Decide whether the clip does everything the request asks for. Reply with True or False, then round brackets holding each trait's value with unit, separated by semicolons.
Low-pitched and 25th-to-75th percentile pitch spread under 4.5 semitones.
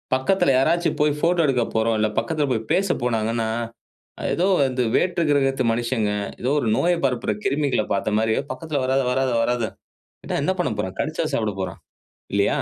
False (130 Hz; 4.9 semitones)